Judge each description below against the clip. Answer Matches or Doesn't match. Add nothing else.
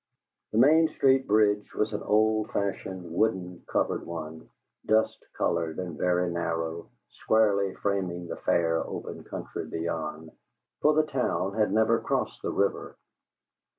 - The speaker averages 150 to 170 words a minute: Doesn't match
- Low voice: Matches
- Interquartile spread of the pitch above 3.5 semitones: Matches